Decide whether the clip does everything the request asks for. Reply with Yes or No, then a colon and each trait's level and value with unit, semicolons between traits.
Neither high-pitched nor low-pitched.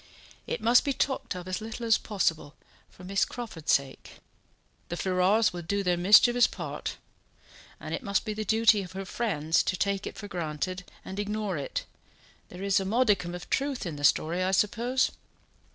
No: high, 195 Hz